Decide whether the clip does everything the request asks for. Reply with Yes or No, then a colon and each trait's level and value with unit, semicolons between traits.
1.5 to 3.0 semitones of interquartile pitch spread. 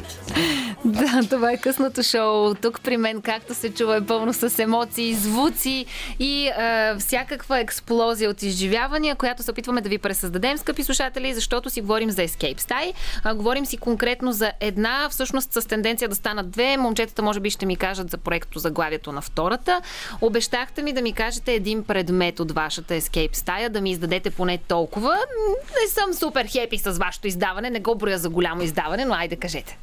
No: average, 4.4 semitones